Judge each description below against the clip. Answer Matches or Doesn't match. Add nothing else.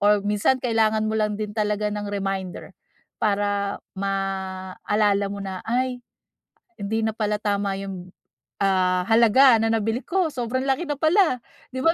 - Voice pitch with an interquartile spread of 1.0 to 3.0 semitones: Matches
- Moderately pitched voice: Doesn't match